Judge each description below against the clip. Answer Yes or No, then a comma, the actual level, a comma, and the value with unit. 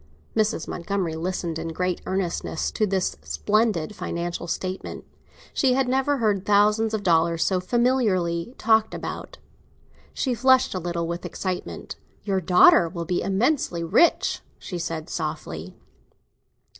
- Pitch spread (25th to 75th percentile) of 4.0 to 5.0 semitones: Yes, average, 4.4 semitones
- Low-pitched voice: No, medium, 185 Hz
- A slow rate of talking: Yes, slow, 130 wpm